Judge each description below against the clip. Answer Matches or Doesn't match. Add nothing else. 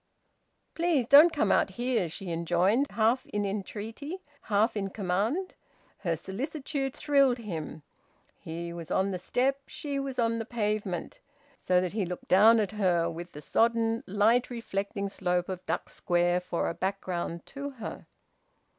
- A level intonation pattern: Doesn't match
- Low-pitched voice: Doesn't match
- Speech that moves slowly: Doesn't match